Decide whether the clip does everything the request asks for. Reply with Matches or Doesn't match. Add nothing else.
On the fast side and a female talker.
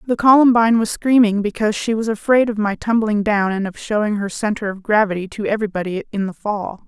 Matches